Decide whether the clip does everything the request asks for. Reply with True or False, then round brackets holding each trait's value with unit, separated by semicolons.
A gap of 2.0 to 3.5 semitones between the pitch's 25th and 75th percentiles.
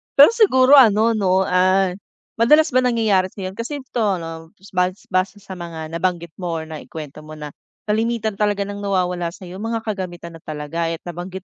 False (4.4 semitones)